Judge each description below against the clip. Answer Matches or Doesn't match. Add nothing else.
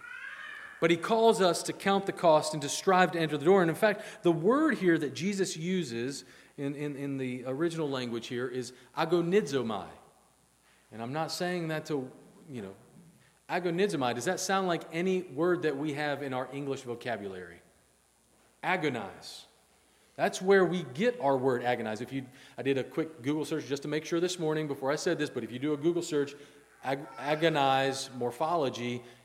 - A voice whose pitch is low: Doesn't match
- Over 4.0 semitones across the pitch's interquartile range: Matches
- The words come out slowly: Doesn't match